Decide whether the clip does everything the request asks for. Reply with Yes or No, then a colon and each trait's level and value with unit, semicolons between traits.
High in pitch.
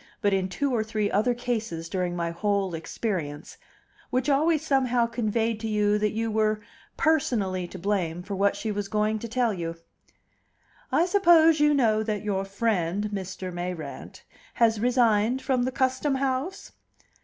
Yes: high, 215 Hz